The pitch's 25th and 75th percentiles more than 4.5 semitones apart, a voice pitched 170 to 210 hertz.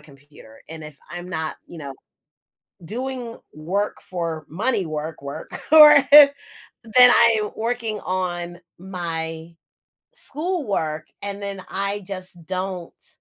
Yes: average, 5.3 semitones; medium, 185 Hz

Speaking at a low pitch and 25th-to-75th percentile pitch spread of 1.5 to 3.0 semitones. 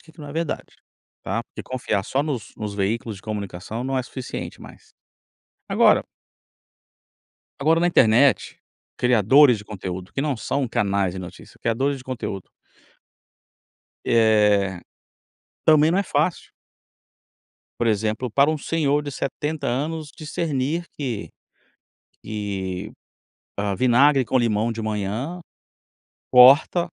No: low, 125 Hz; wide, 5.6 semitones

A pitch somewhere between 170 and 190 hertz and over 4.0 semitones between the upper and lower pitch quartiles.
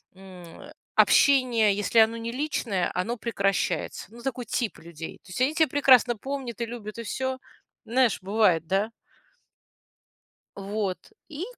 No: high, 230 Hz; average, 4.5 semitones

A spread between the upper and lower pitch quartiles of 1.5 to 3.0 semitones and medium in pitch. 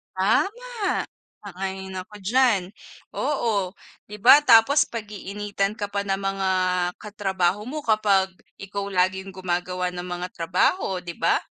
No: narrow, 2.4 semitones; high, 195 Hz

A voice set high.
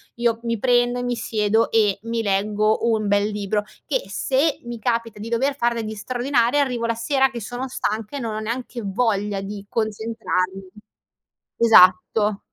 Yes: high, 225 Hz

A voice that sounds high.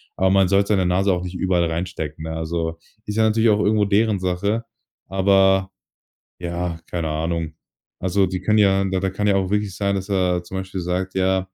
No: very low, 95 Hz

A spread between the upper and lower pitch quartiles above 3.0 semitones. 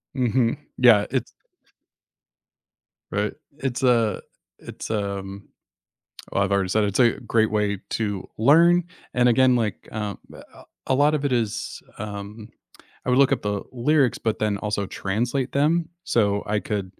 Yes: average, 3.9 semitones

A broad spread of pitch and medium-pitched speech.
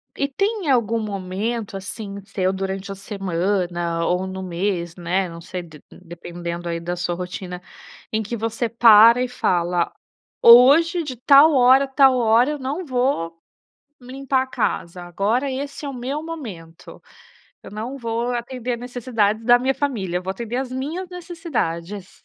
No: wide, 6.1 semitones; high, 225 Hz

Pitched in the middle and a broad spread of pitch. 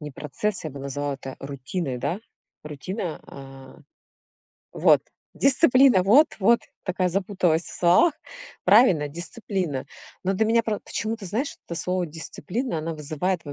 Yes: medium, 180 Hz; wide, 6.1 semitones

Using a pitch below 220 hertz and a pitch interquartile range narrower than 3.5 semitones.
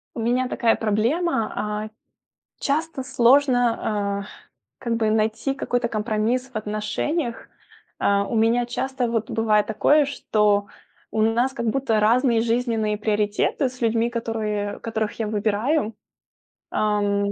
No: high, 225 Hz; average, 2.7 semitones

